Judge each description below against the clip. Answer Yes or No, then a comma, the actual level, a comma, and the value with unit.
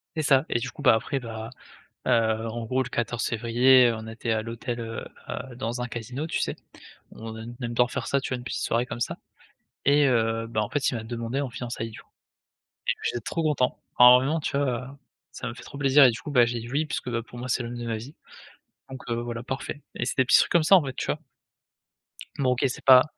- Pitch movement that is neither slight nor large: No, narrow, 2.3 semitones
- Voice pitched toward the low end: Yes, low, 125 Hz